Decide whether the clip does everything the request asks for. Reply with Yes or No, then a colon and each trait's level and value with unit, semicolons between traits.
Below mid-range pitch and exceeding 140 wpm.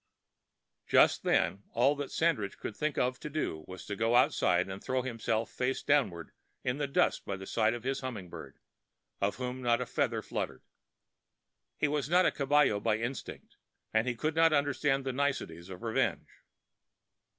Yes: low, 125 Hz; average, 175 wpm